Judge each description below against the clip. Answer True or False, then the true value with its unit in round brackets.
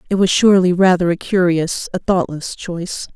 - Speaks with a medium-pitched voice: True (180 Hz)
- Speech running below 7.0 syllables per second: True (5.3 syllables/s)